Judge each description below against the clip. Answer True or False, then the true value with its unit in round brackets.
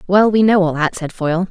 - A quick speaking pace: True (280 wpm)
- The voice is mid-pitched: True (180 Hz)